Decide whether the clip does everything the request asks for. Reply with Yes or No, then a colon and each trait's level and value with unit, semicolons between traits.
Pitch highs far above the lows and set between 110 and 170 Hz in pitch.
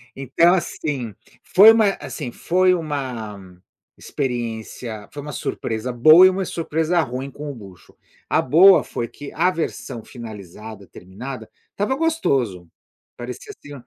Yes: wide, 6.9 semitones; low, 135 Hz